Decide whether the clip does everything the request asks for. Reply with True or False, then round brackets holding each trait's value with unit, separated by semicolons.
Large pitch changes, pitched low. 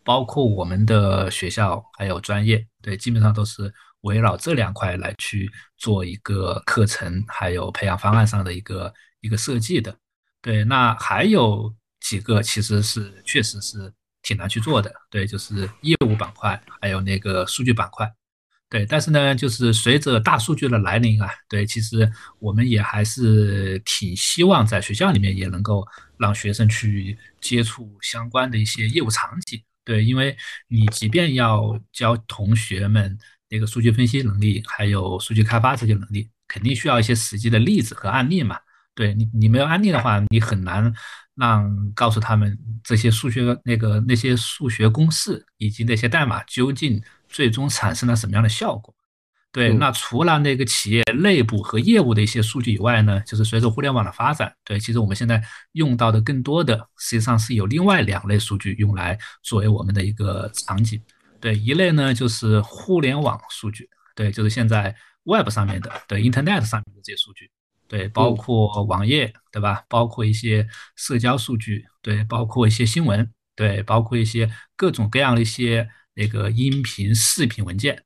False (2.5 semitones; 110 Hz)